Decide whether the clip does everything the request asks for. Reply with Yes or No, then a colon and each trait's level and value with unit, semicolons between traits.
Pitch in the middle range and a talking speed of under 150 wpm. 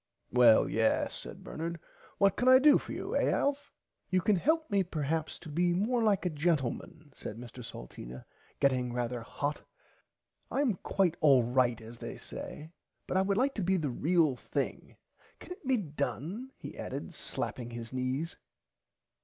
No: medium, 160 Hz; average, 170 wpm